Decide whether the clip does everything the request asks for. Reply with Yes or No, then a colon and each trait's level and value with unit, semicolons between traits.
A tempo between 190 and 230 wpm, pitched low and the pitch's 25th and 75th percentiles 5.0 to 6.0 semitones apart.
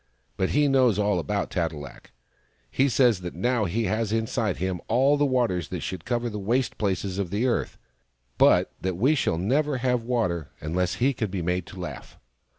Yes: average, 200 wpm; low, 105 Hz; wide, 5.5 semitones